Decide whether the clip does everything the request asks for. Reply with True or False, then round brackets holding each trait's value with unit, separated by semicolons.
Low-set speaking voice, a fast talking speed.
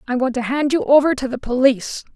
False (260 Hz; 250 wpm)